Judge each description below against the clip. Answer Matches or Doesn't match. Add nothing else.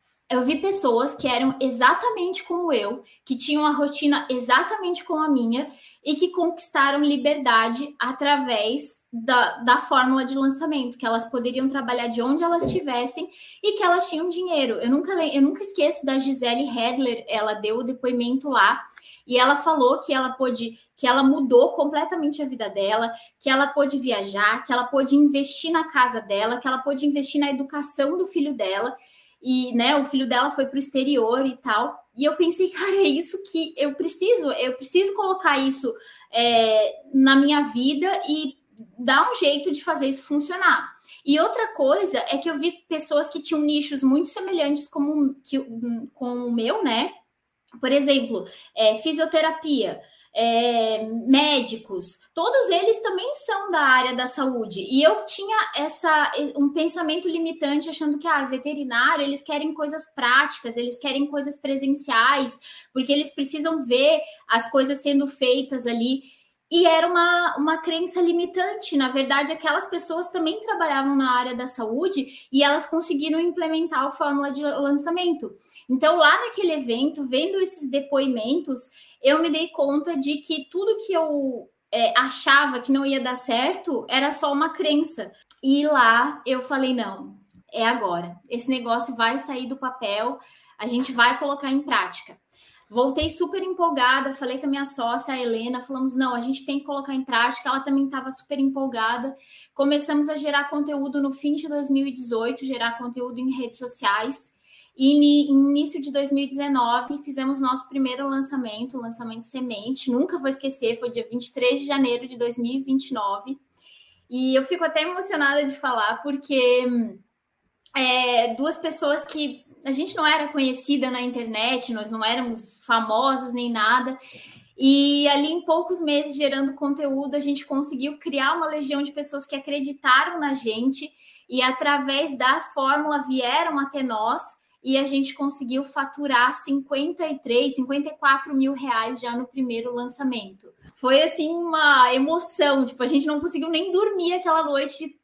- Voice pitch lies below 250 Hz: Doesn't match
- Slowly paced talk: Doesn't match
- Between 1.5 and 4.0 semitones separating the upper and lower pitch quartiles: Matches